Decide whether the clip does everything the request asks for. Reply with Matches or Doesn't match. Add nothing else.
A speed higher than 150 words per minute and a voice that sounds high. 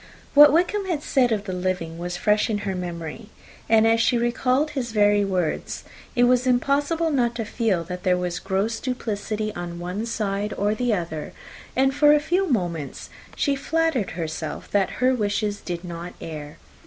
Matches